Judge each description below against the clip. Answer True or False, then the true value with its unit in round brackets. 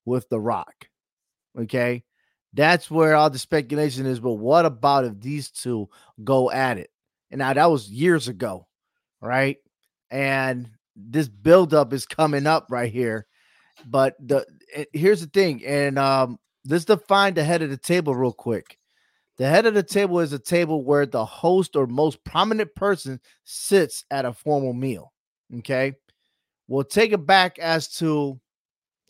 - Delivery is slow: False (160 wpm)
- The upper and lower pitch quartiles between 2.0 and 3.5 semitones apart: False (4.6 semitones)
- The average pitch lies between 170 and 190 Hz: False (140 Hz)